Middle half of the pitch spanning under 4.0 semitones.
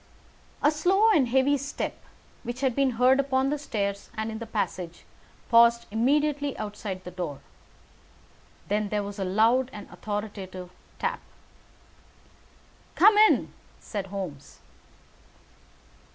No: wide, 5.5 semitones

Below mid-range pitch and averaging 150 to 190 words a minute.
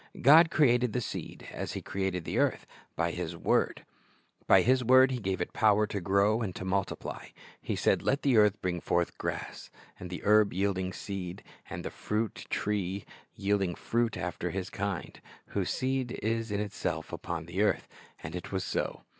Yes: low, 100 Hz; average, 175 wpm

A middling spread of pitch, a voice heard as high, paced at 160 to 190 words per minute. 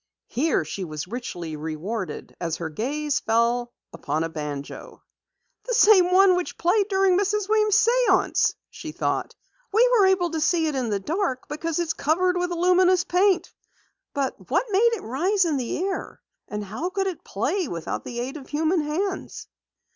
No: wide, 8.4 semitones; very high, 325 Hz; average, 170 wpm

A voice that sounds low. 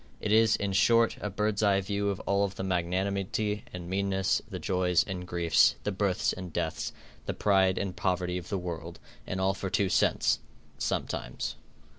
Yes: very low, 95 Hz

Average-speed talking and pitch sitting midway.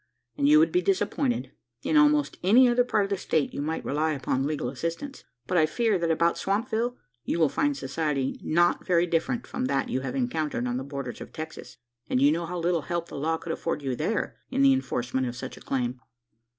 No: fast, 220 wpm; medium, 165 Hz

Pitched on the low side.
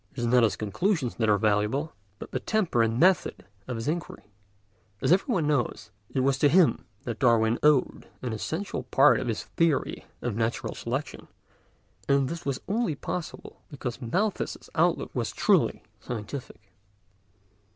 Yes: low, 130 Hz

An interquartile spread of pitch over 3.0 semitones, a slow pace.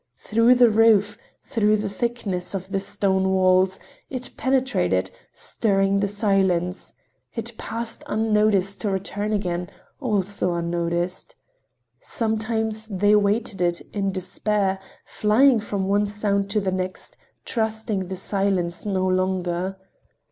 No: narrow, 2.5 semitones; slow, 120 wpm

